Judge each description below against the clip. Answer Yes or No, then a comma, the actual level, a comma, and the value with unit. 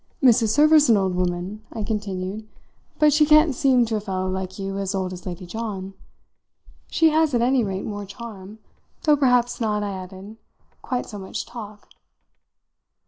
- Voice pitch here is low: No, high, 210 Hz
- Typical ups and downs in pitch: Yes, average, 4.5 semitones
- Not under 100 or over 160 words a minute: No, average, 170 wpm